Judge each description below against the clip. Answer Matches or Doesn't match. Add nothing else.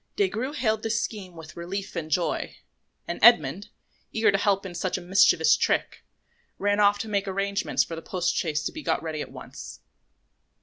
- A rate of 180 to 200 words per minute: Matches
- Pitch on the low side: Doesn't match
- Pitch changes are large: Doesn't match